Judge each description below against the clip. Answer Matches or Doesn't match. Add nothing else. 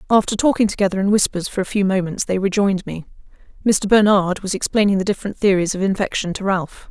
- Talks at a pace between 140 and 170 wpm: Doesn't match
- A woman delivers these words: Matches